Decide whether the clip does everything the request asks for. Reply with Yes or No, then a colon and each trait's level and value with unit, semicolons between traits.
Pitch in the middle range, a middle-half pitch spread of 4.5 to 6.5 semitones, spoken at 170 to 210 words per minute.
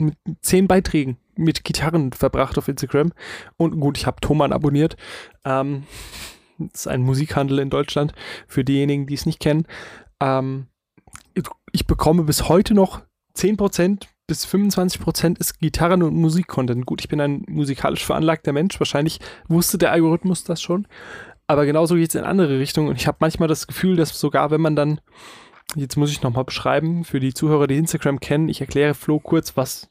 No: medium, 150 Hz; average, 2.9 semitones; average, 175 wpm